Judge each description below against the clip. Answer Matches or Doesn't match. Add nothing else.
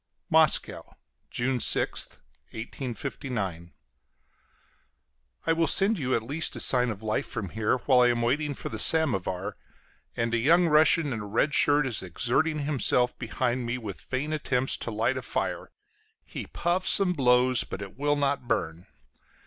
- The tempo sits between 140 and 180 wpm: Matches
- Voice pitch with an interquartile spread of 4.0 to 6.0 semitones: Matches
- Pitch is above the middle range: Doesn't match